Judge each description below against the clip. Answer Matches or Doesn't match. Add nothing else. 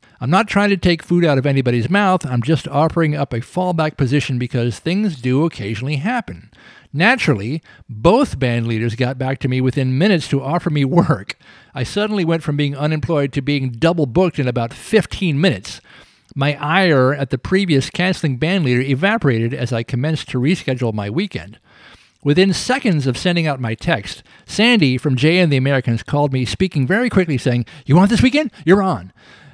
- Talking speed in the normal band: Matches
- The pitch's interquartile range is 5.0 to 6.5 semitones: Matches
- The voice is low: Doesn't match